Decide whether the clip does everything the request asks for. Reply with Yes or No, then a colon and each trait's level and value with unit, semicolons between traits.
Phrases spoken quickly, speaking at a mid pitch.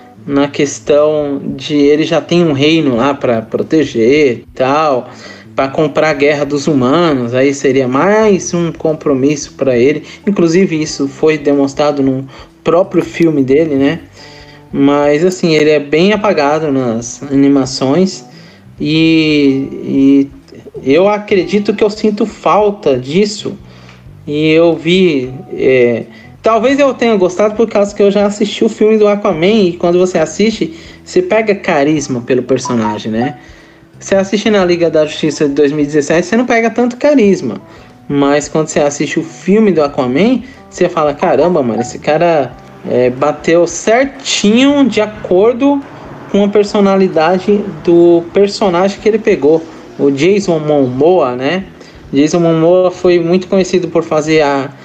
No: average, 145 wpm; medium, 160 Hz